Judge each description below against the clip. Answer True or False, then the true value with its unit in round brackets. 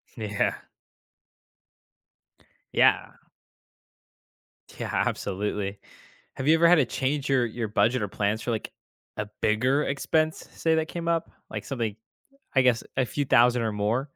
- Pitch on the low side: True (125 Hz)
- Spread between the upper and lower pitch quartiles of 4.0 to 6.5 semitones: True (5.1 semitones)